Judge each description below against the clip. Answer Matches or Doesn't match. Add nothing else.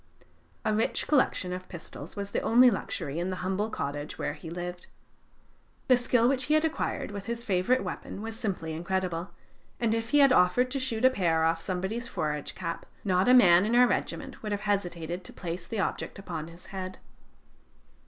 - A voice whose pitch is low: Doesn't match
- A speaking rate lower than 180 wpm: Doesn't match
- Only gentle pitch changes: Doesn't match